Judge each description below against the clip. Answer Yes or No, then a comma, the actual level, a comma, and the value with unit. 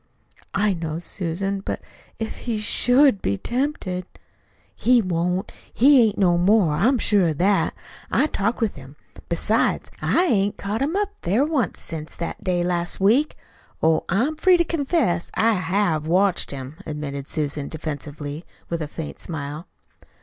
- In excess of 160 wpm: No, average, 155 wpm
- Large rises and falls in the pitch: Yes, wide, 6.1 semitones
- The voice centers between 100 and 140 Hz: No, medium, 185 Hz